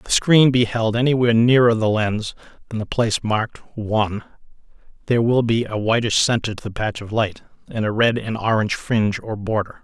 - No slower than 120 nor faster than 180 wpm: No, average, 200 wpm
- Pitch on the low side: Yes, low, 110 Hz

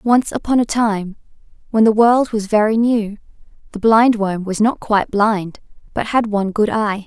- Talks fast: No, average, 180 wpm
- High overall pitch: Yes, high, 215 Hz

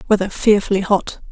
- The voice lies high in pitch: Yes, high, 200 Hz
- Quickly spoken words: No, slow, 135 wpm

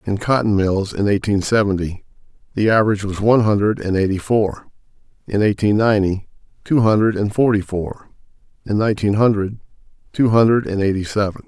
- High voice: No, low, 105 Hz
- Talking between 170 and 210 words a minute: No, average, 155 wpm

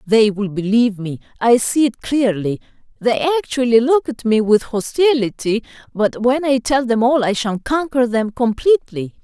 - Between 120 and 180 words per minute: Yes, average, 170 wpm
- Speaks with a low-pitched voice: No, high, 235 Hz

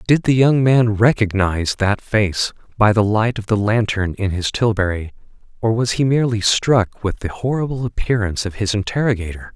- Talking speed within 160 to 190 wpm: Yes, average, 175 wpm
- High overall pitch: No, low, 105 Hz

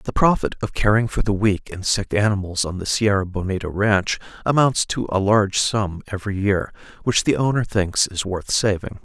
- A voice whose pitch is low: Yes, low, 100 Hz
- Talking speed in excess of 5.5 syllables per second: No, 5.1 syllables/s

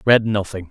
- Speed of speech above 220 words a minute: Yes, fast, 255 wpm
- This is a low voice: Yes, low, 105 Hz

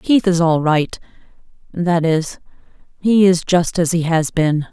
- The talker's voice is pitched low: No, medium, 170 Hz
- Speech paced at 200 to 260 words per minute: No, average, 155 wpm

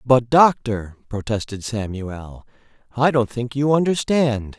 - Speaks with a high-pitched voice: No, low, 120 Hz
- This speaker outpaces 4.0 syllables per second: No, 3.9 syllables/s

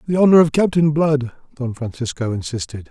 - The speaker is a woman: No, male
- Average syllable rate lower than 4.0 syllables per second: No, 5.6 syllables/s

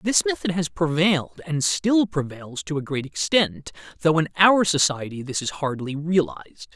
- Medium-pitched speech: Yes, medium, 155 Hz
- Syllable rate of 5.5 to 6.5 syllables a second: No, 4.7 syllables/s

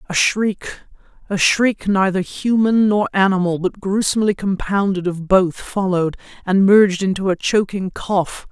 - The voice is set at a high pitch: Yes, high, 195 Hz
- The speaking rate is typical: No, slow, 125 wpm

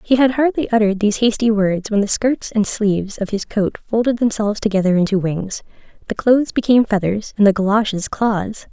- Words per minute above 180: Yes, average, 195 wpm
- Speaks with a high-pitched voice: Yes, high, 215 Hz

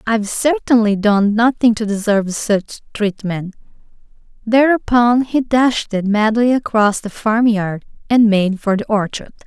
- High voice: Yes, high, 220 Hz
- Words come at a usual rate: No, slow, 125 wpm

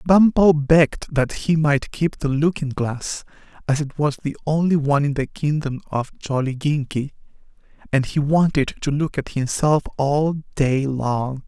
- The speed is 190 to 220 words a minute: No, average, 155 wpm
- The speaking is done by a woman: No, male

